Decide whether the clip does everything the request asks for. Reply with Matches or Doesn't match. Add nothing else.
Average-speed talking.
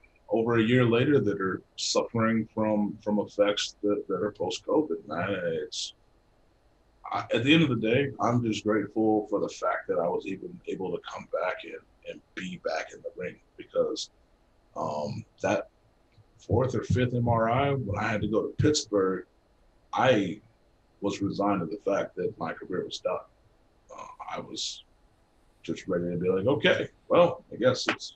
Matches